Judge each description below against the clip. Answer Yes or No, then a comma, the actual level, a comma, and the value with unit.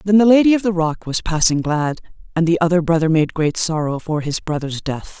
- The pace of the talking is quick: Yes, fast, 230 wpm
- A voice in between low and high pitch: Yes, medium, 170 Hz